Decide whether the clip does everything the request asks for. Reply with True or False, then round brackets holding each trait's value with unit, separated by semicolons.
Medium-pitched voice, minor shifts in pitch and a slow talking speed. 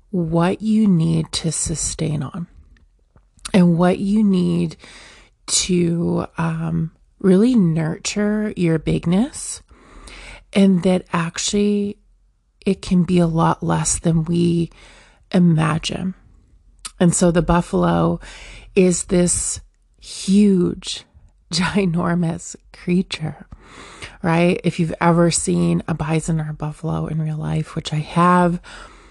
True (170 Hz; 2.3 semitones; 110 wpm)